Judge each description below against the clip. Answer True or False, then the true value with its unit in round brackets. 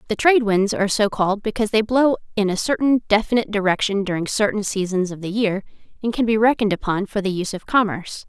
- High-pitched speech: True (210 Hz)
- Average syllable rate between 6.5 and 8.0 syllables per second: True (6.7 syllables/s)